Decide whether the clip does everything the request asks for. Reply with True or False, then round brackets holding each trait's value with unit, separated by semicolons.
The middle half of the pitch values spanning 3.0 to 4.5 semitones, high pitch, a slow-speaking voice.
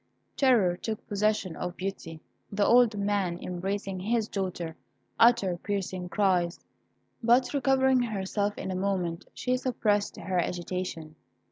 True (3.6 semitones; 195 Hz; 125 wpm)